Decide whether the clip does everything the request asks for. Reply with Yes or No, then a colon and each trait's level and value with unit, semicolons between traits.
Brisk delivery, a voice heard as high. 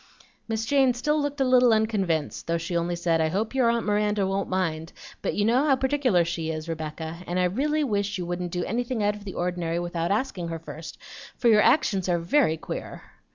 Yes: fast, 215 wpm; high, 195 Hz